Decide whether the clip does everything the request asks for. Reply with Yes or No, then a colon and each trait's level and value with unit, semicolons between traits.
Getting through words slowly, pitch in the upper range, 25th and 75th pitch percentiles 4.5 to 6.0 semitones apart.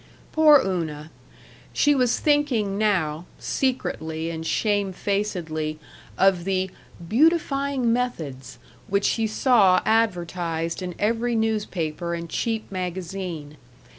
Yes: slow, 100 wpm; high, 195 Hz; wide, 5.4 semitones